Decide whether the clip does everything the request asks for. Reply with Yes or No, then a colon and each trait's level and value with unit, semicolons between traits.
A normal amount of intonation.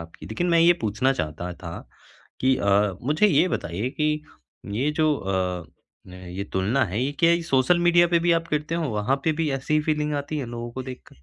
No: wide, 7.5 semitones